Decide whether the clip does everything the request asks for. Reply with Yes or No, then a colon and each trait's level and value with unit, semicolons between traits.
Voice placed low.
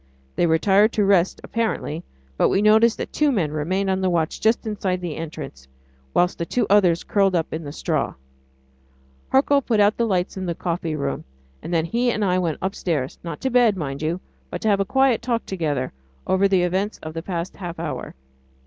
No: medium, 185 Hz